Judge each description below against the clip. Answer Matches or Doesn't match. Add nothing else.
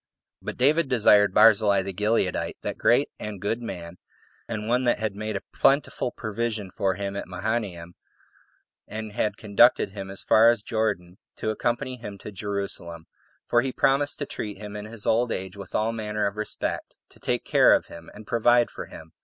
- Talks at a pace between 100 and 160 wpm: Doesn't match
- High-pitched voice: Doesn't match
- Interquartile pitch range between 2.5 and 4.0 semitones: Matches